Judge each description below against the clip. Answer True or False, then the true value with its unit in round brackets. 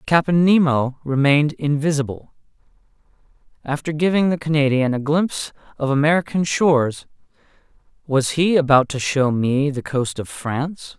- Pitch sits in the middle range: True (145 Hz)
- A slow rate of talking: True (125 wpm)